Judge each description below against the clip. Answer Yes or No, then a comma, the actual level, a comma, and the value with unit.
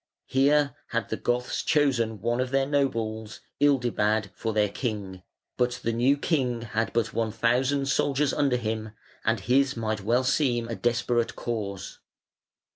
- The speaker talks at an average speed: Yes, average, 150 wpm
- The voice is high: No, low, 120 Hz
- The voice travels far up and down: No, average, 3.4 semitones